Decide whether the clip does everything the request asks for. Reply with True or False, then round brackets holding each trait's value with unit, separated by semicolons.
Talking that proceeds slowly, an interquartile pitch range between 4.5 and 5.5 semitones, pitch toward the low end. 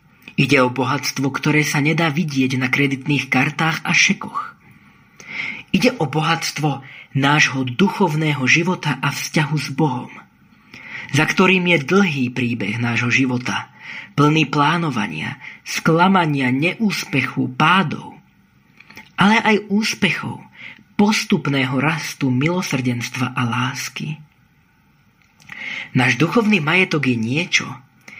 False (100 wpm; 5.2 semitones; 150 Hz)